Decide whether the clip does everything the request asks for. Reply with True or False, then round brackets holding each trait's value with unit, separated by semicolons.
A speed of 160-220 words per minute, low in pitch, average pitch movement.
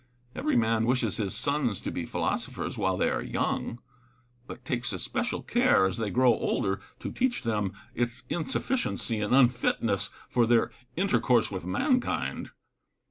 False (150 wpm; 120 Hz; 3.4 semitones)